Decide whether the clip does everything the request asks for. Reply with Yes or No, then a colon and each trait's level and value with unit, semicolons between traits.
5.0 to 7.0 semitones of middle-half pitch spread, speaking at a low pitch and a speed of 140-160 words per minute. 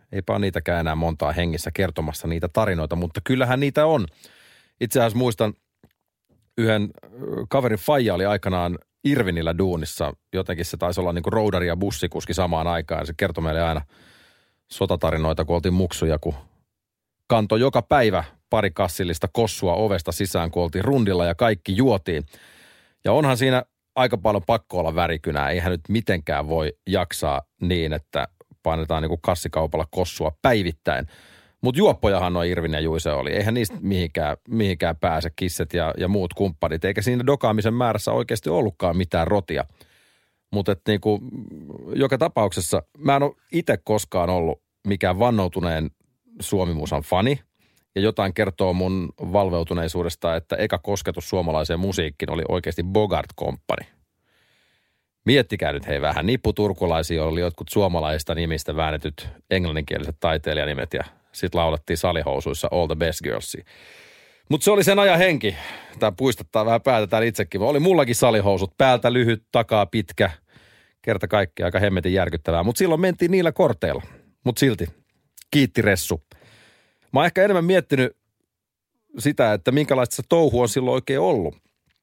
Yes: average, 5.3 semitones; very low, 95 Hz; average, 145 wpm